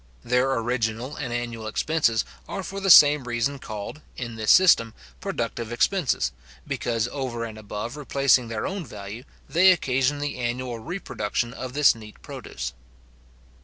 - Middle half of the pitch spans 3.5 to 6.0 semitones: Yes, average, 4.1 semitones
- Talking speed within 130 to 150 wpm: Yes, average, 145 wpm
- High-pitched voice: No, low, 125 Hz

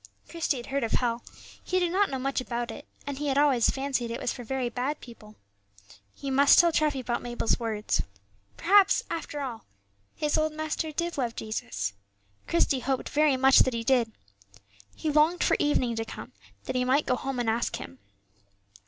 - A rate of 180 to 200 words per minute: Yes, average, 190 wpm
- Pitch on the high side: Yes, very high, 265 Hz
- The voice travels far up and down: No, average, 3.9 semitones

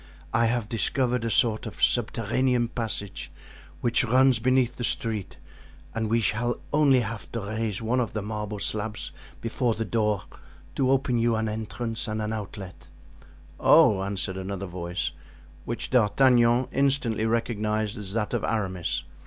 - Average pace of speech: Yes, average, 150 wpm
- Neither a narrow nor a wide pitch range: No, narrow, 2.3 semitones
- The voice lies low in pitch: Yes, low, 115 Hz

